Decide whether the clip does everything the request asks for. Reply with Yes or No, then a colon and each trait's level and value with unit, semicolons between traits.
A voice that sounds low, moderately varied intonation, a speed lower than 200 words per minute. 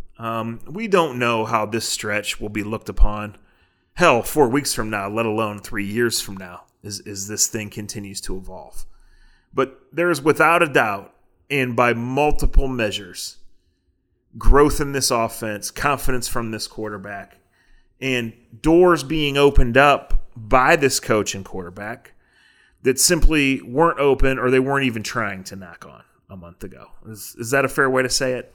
Yes: low, 115 Hz; average, 4.6 semitones; average, 170 wpm